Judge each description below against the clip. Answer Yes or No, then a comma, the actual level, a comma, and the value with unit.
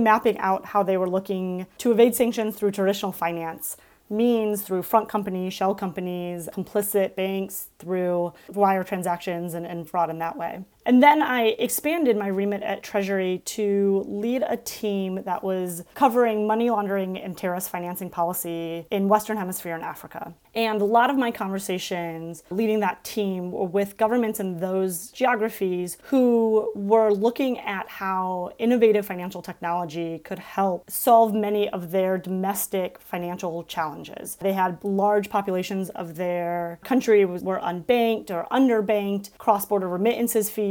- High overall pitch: Yes, high, 195 Hz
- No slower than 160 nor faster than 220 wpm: No, average, 150 wpm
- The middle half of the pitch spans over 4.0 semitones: No, average, 3.1 semitones